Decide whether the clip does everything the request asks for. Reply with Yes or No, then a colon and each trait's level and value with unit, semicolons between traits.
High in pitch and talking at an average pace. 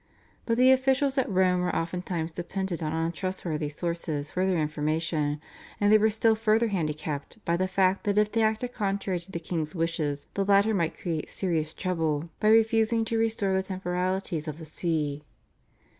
No: medium, 180 Hz; average, 175 wpm